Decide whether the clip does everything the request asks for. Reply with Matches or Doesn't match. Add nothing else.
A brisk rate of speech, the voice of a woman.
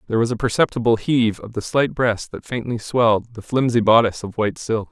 Doesn't match